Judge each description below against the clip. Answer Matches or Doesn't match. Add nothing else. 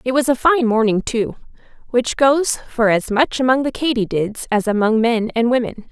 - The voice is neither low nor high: Doesn't match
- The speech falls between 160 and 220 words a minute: Matches